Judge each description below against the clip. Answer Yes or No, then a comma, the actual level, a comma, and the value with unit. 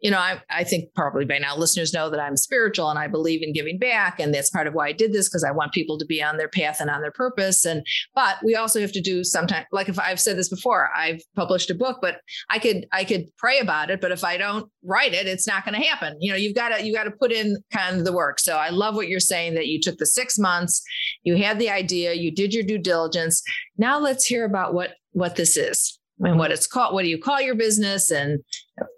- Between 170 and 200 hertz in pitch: Yes, medium, 185 Hz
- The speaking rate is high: Yes, fast, 270 wpm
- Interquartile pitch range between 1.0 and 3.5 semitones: No, average, 4.6 semitones